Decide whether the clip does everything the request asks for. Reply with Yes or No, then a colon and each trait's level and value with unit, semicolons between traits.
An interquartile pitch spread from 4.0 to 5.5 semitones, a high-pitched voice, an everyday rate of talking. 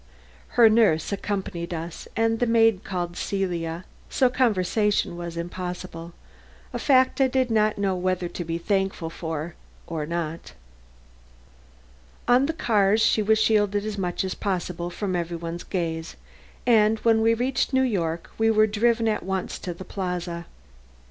Yes: average, 4.4 semitones; high, 195 Hz; average, 155 wpm